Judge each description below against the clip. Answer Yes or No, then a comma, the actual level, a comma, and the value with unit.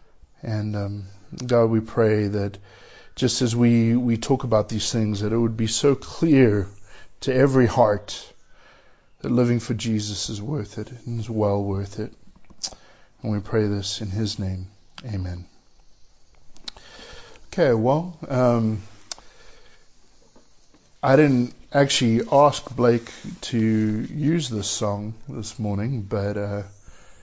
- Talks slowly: Yes, slow, 130 wpm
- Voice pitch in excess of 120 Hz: No, low, 110 Hz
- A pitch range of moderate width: Yes, average, 3.0 semitones